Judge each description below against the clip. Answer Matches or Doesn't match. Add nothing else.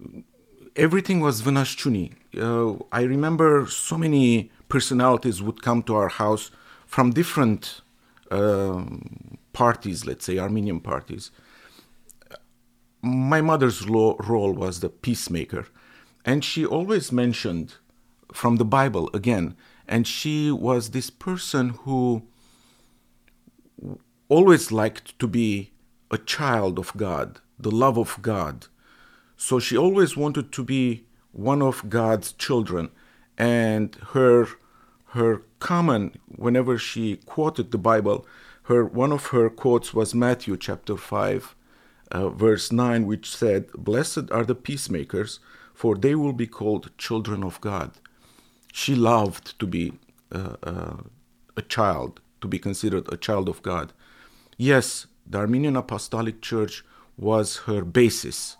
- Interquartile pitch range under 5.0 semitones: Matches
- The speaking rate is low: Matches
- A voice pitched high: Doesn't match